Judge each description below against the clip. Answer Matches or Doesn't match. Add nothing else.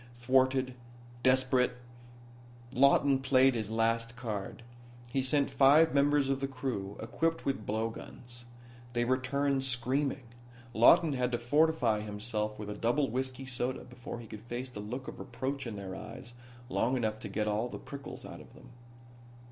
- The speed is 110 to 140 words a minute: Doesn't match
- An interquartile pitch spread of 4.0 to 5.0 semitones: Doesn't match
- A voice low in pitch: Matches